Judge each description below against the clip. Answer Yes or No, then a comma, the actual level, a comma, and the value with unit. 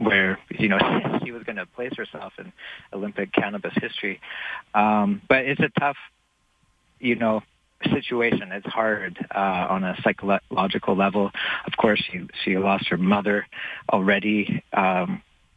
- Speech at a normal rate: Yes, average, 145 wpm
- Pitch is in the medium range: No, low, 105 Hz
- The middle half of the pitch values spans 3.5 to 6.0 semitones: No, narrow, 2.4 semitones